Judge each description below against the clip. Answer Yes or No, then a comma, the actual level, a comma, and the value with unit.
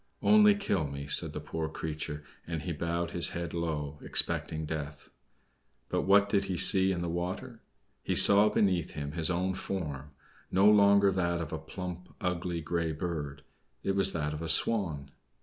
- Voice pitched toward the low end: Yes, very low, 85 Hz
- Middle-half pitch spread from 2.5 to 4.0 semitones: Yes, average, 3.5 semitones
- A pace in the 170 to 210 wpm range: Yes, average, 175 wpm